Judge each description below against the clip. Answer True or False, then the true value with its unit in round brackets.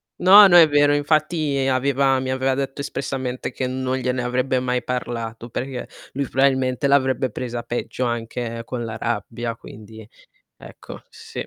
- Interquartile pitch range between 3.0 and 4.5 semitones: False (2.4 semitones)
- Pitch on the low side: True (130 Hz)